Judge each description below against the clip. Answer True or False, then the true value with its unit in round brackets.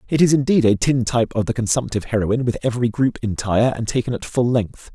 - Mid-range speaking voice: False (120 Hz)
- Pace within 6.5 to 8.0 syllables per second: True (6.6 syllables/s)